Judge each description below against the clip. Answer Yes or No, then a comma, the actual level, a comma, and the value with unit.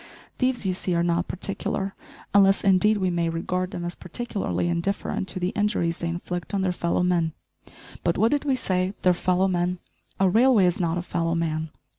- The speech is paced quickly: No, average, 195 wpm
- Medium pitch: Yes, medium, 180 Hz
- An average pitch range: No, narrow, 2.3 semitones